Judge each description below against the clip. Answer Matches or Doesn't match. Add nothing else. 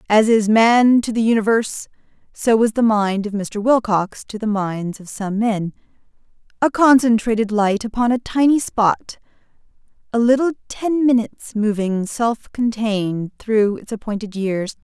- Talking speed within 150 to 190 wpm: Doesn't match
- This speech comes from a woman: Matches